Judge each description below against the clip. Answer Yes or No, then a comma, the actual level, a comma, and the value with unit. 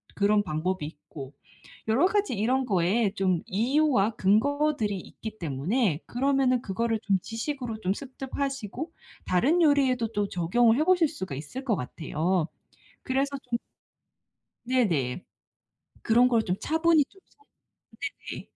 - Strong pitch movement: Yes, wide, 6.4 semitones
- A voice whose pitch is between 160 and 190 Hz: No, high, 225 Hz